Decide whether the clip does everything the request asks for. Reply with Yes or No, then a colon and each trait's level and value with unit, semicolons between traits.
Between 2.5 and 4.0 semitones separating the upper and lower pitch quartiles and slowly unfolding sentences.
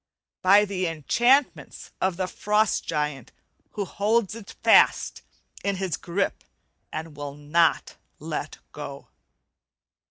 No: average, 4.6 semitones; slow, 120 wpm